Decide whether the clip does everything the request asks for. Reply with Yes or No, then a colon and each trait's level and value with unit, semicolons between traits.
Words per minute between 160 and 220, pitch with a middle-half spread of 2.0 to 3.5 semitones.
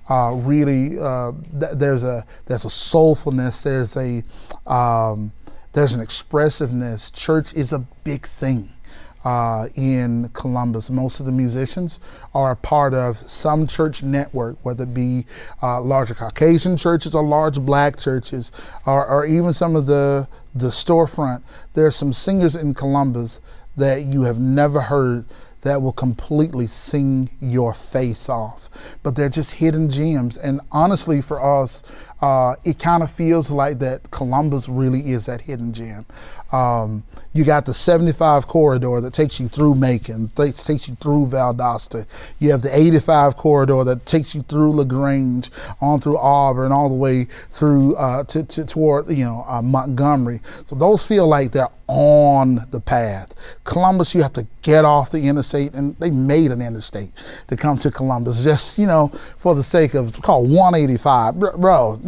Yes: average, 165 wpm; average, 3.2 semitones